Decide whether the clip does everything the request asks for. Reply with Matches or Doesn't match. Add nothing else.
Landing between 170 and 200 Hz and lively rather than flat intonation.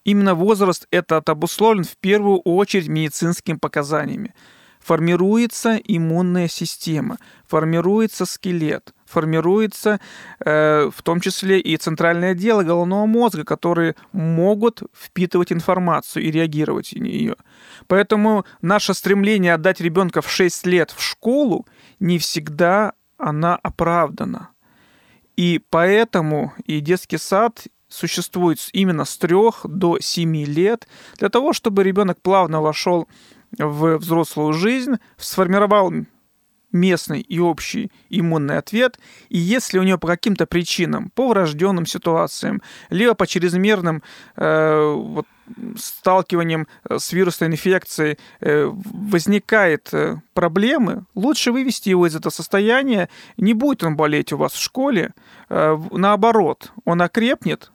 Doesn't match